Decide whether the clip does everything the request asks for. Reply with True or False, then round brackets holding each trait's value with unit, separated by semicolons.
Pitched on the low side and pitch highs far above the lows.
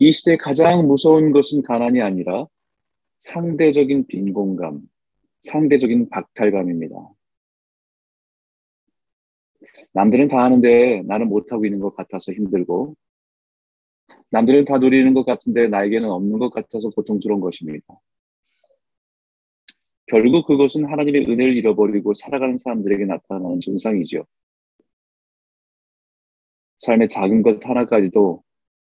True (120 Hz; 6.1 semitones)